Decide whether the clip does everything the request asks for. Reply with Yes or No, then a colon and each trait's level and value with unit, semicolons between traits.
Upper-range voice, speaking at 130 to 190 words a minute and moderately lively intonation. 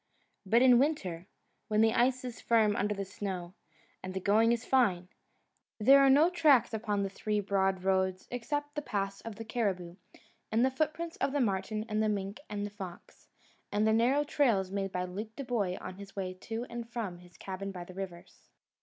No: high, 210 Hz; average, 200 wpm; average, 4.0 semitones